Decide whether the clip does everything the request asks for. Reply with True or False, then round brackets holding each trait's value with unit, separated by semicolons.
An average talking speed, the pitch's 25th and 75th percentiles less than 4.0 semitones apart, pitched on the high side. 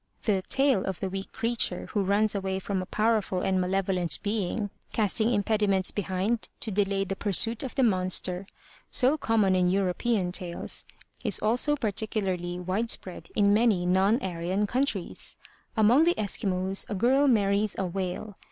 True (155 wpm; 2.9 semitones; 200 Hz)